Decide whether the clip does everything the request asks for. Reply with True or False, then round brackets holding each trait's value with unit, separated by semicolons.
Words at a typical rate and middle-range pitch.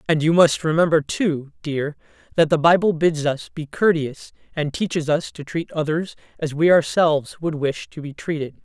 True (190 wpm; 155 Hz)